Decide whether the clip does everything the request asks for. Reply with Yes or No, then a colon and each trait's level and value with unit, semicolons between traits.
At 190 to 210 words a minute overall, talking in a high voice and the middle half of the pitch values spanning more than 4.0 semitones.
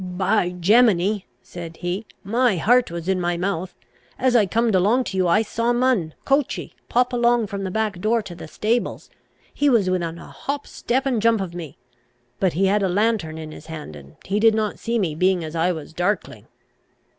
Yes: fast, 205 wpm; high, 195 Hz; average, 4.7 semitones